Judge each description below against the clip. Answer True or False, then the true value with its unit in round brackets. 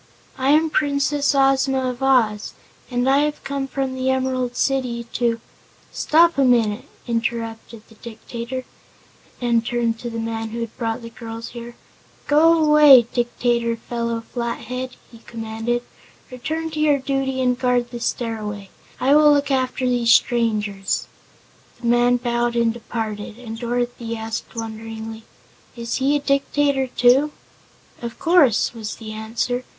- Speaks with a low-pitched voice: False (240 Hz)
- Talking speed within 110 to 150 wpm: True (145 wpm)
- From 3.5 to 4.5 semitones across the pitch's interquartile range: False (2.7 semitones)